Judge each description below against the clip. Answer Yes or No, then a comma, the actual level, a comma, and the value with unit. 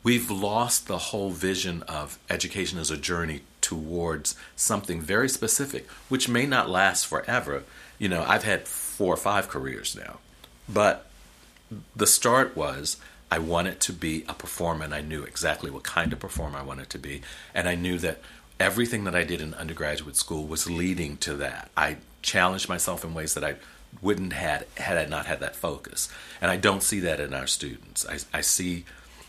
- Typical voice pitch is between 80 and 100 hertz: Yes, very low, 85 Hz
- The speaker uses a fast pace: No, average, 185 wpm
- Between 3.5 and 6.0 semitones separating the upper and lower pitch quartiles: Yes, average, 3.9 semitones